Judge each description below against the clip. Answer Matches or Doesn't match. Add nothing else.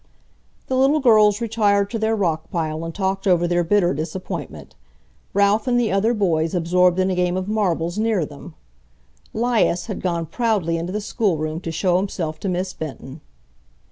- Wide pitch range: Doesn't match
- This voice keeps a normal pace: Matches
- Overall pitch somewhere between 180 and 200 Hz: Matches